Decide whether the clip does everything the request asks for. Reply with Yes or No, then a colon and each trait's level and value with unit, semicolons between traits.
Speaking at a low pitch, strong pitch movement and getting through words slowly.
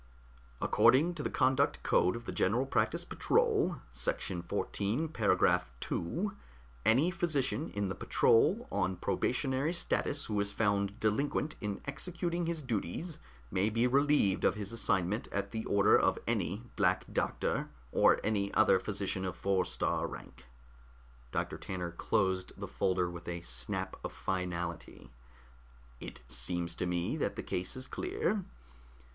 No: low, 100 Hz; wide, 7.1 semitones; average, 145 wpm